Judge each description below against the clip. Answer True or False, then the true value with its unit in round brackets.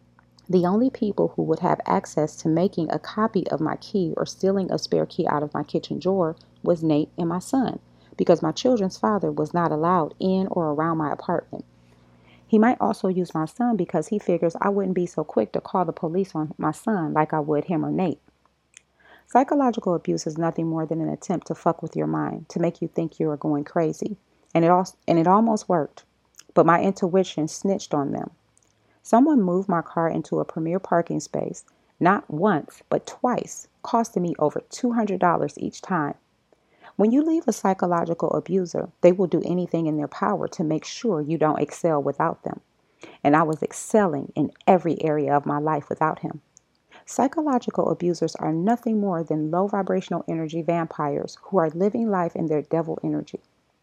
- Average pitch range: True (3.6 semitones)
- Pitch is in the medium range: True (170 Hz)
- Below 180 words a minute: False (190 wpm)